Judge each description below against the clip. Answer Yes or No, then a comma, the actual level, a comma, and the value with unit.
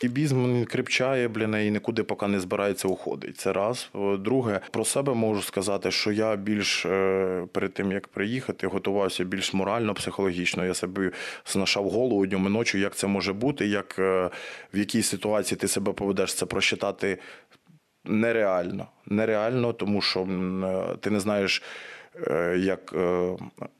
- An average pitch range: No, narrow, 2.3 semitones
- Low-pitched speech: Yes, low, 100 Hz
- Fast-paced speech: No, average, 140 wpm